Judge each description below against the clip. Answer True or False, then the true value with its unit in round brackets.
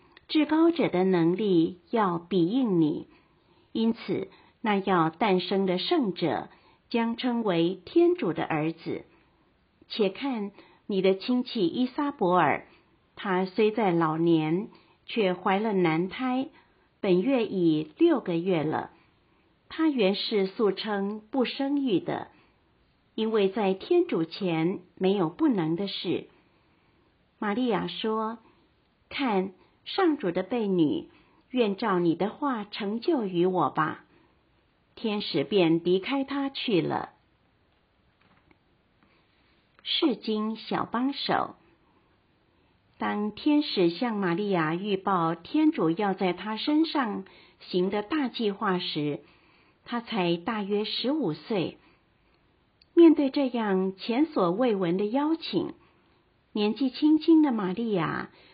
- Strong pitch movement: True (6.1 semitones)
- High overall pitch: True (210 Hz)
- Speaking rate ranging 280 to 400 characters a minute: False (160 characters per minute)